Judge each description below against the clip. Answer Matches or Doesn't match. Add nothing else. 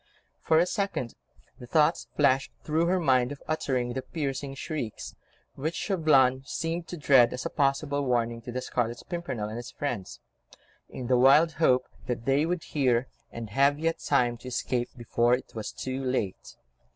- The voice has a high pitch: Doesn't match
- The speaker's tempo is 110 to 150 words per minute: Doesn't match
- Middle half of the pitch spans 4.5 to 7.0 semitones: Doesn't match